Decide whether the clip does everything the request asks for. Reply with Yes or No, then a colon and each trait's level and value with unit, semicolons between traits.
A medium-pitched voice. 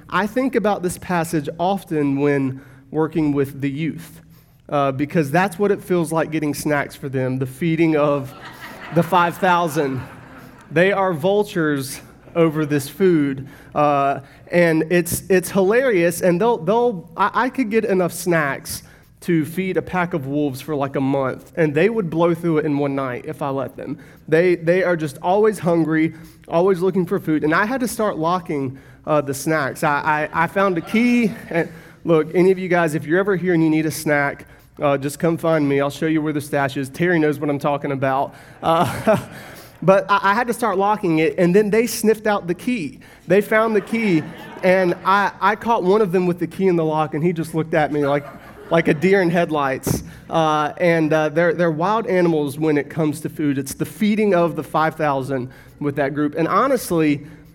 Yes: medium, 160 Hz